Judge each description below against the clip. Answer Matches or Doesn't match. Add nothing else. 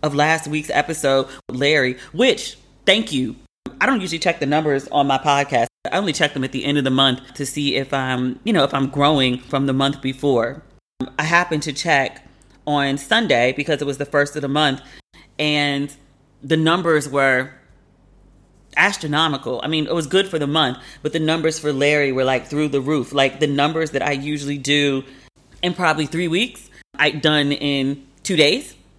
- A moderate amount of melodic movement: Doesn't match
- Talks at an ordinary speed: Matches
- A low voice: Doesn't match